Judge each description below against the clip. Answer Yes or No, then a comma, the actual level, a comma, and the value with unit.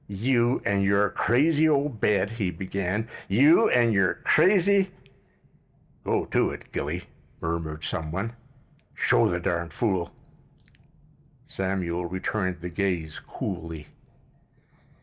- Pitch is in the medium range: No, low, 100 Hz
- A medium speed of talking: No, slow, 110 wpm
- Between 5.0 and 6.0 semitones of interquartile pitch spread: Yes, wide, 5.4 semitones